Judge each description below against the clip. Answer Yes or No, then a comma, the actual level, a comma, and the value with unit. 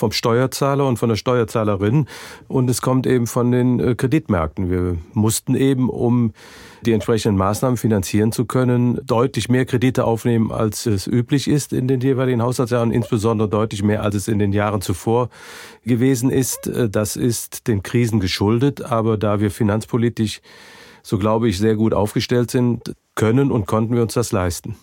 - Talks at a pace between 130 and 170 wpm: Yes, average, 165 wpm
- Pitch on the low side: Yes, low, 115 Hz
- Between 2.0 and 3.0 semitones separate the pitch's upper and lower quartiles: Yes, average, 2.7 semitones